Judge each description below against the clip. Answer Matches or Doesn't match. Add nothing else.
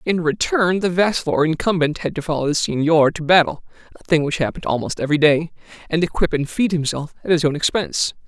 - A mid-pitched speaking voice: Matches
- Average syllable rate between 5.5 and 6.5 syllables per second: Doesn't match